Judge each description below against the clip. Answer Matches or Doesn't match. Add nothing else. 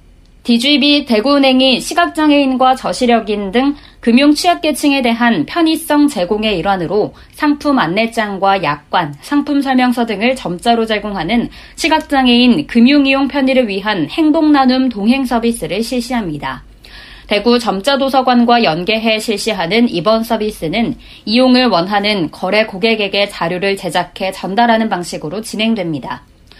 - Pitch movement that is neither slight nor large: Matches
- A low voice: Doesn't match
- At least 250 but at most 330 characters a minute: Matches